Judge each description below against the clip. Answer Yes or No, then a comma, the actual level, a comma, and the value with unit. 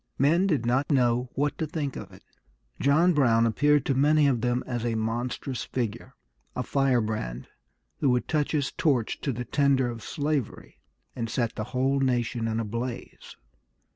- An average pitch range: Yes, average, 3.3 semitones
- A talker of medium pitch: No, low, 125 Hz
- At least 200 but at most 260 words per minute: No, average, 170 wpm